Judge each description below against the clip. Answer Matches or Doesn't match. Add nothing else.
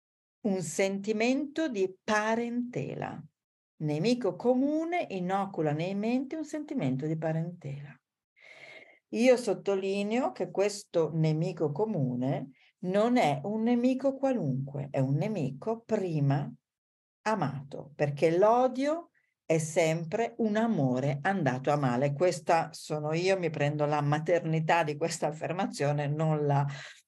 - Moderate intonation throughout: Doesn't match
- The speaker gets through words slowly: Matches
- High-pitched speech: Doesn't match